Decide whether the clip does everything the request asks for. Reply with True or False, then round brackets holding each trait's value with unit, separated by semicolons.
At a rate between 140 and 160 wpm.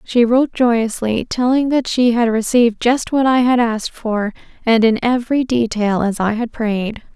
False (185 wpm)